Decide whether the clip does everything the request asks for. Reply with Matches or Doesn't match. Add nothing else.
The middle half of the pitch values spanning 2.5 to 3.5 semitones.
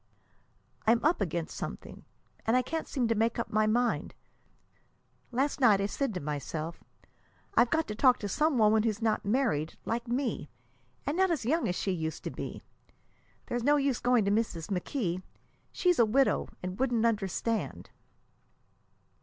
Doesn't match